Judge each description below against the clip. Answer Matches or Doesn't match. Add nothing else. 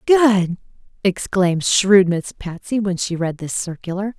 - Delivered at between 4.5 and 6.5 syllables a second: Doesn't match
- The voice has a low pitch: Doesn't match